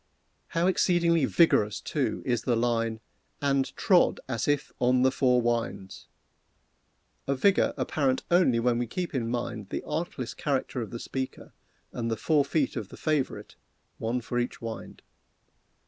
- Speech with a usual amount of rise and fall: Yes, average, 3.8 semitones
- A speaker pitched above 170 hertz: No, low, 125 Hz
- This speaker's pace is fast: No, average, 155 wpm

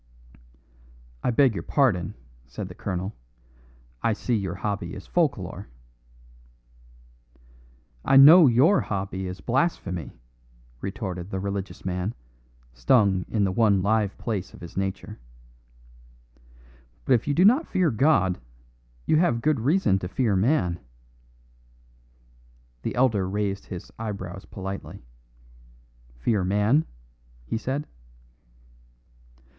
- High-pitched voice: No, low, 105 Hz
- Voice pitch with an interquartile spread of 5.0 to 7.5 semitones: Yes, average, 5.3 semitones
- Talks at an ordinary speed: No, slow, 115 wpm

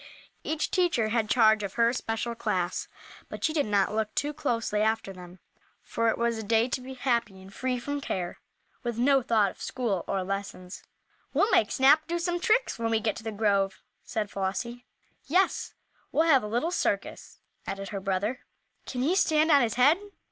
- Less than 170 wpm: No, average, 190 wpm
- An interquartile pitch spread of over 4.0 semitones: Yes, average, 4.9 semitones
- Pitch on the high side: Yes, high, 230 Hz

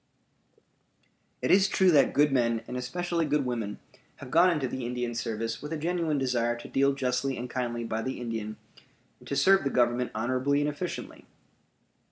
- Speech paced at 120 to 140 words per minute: No, average, 180 wpm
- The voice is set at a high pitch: No, low, 130 Hz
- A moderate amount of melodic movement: Yes, average, 3.9 semitones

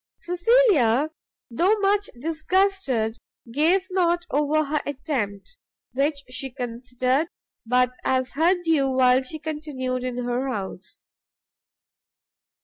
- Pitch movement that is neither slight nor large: Yes, average, 4.7 semitones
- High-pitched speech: Yes, very high, 280 Hz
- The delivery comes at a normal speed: No, slow, 105 wpm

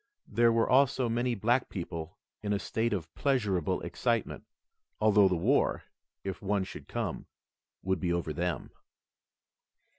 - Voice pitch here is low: Yes, low, 100 Hz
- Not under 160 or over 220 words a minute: No, average, 140 wpm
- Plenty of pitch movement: No, average, 4.8 semitones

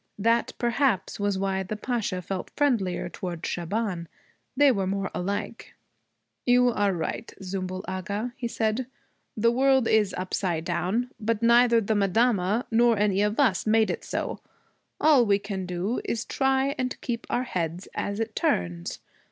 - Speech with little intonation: No, average, 4.1 semitones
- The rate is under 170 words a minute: Yes, average, 155 wpm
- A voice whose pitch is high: Yes, high, 210 Hz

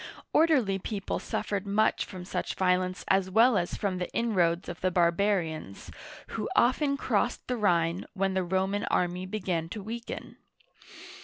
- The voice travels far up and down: No, average, 2.9 semitones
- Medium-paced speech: Yes, average, 155 wpm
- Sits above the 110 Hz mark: Yes, high, 190 Hz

